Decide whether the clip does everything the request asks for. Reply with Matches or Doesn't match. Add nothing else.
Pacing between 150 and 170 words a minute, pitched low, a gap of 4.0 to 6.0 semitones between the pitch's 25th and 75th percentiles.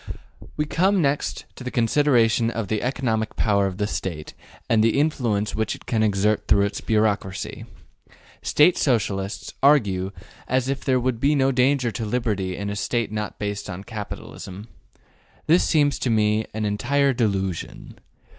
Matches